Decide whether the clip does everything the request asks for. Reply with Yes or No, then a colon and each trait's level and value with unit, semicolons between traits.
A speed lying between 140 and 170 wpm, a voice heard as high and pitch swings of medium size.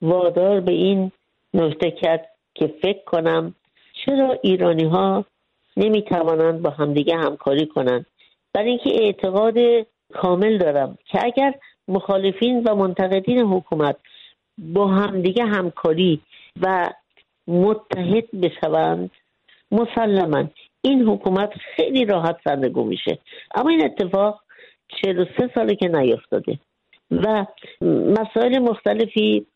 No: slow, 105 wpm; high, 195 Hz; average, 4.3 semitones